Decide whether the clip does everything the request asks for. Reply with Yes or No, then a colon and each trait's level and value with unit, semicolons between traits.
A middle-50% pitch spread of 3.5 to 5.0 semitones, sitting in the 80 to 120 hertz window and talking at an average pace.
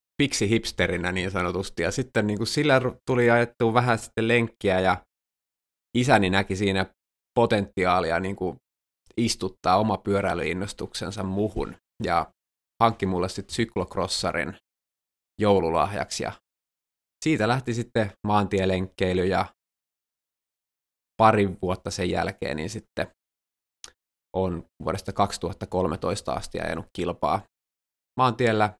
Yes: average, 3.9 semitones; very low, 95 Hz; average, 105 wpm